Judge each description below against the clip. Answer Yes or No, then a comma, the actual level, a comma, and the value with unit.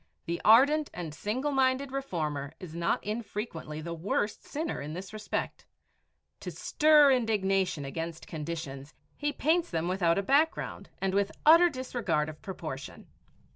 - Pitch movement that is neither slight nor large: No, wide, 8.5 semitones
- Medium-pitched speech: No, high, 195 Hz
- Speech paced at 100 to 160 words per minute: Yes, average, 140 wpm